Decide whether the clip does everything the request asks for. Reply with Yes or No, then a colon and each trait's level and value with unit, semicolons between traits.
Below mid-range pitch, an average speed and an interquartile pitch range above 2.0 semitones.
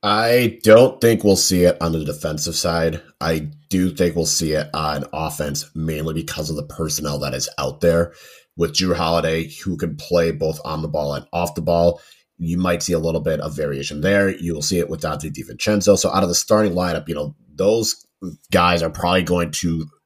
No: very low, 85 Hz; fast, 210 wpm; average, 2.7 semitones